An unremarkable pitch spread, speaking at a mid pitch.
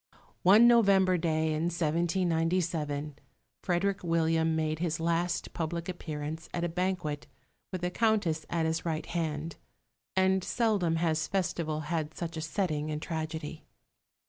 No: narrow, 2.2 semitones; medium, 165 Hz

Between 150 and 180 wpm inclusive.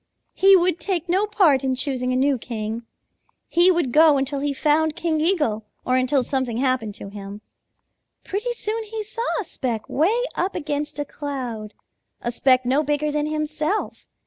Yes: average, 175 wpm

